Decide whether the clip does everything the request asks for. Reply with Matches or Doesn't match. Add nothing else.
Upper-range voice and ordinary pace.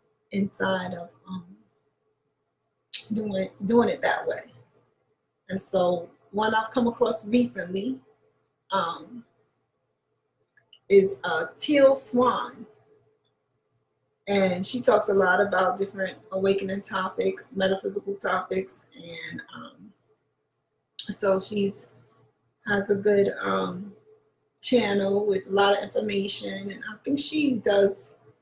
Doesn't match